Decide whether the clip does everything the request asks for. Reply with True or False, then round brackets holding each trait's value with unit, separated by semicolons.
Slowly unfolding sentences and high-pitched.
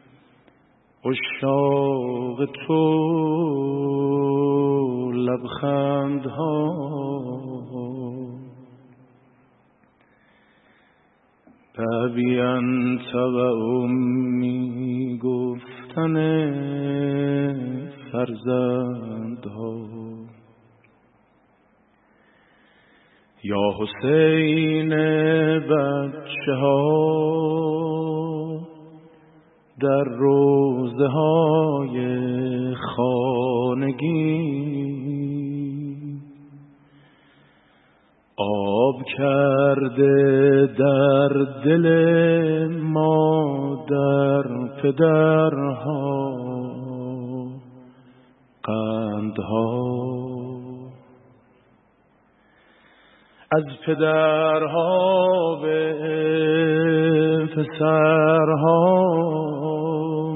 False (30 wpm; 140 Hz)